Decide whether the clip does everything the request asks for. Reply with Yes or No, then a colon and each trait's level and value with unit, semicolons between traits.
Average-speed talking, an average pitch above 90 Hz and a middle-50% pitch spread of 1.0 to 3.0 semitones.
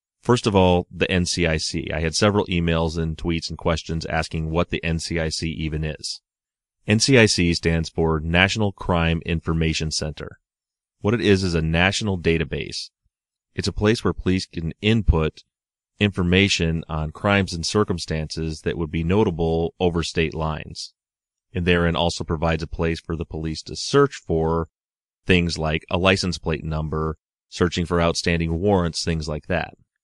No: average, 155 wpm; very low, 85 Hz; narrow, 2.5 semitones